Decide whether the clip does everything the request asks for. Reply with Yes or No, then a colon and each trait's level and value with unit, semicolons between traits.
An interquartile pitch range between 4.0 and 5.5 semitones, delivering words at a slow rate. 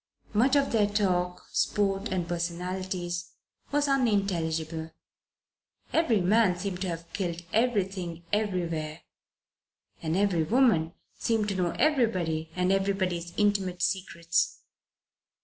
No: average, 3.2 semitones; slow, 110 wpm